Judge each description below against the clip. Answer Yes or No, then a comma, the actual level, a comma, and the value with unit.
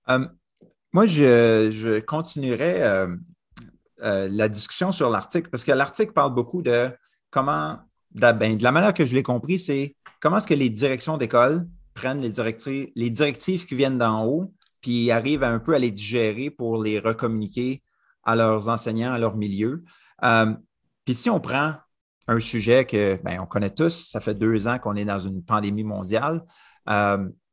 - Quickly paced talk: No, average, 180 wpm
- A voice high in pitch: No, low, 120 Hz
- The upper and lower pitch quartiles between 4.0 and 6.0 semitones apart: Yes, average, 5.3 semitones